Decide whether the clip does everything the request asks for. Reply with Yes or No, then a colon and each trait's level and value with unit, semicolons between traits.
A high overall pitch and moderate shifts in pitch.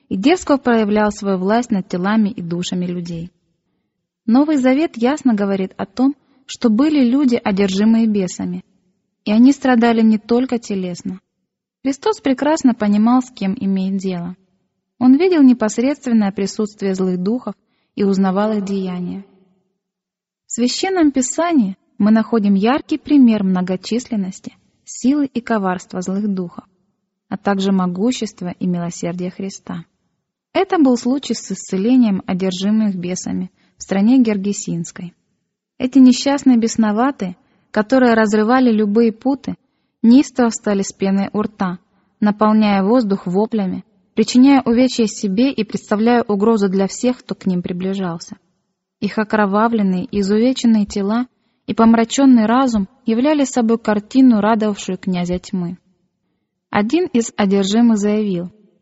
Yes: high, 210 Hz; average, 4.0 semitones